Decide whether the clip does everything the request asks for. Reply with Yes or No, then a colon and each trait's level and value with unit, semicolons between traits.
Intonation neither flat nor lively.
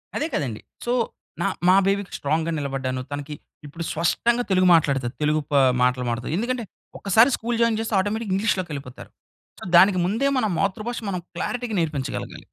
No: wide, 7.5 semitones